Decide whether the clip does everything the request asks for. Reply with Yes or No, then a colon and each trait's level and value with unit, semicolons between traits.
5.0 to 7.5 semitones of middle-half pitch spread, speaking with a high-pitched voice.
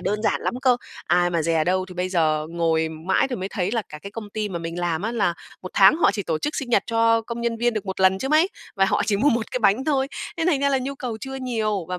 Yes: wide, 5.5 semitones; high, 210 Hz